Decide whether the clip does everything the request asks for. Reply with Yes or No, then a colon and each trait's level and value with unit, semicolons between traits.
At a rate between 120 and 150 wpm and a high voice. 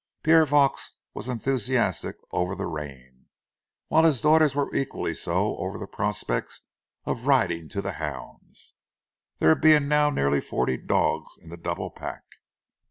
No: average, 145 wpm; low, 120 Hz